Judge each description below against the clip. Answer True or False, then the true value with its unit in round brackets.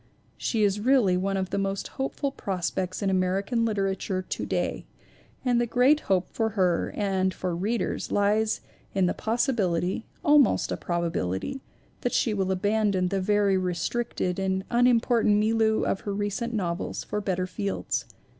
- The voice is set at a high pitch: True (200 Hz)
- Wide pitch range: False (3.3 semitones)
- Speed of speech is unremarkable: True (160 wpm)